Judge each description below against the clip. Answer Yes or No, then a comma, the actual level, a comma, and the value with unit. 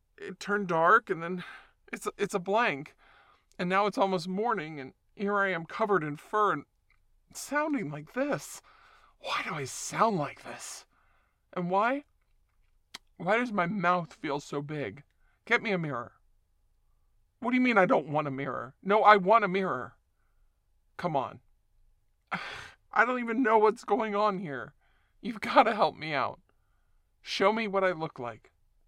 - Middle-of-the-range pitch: Yes, medium, 180 Hz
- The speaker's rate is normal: Yes, average, 165 wpm